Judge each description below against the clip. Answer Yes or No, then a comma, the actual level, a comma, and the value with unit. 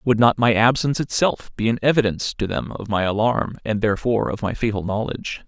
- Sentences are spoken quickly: Yes, fast, 210 wpm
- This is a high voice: No, low, 115 Hz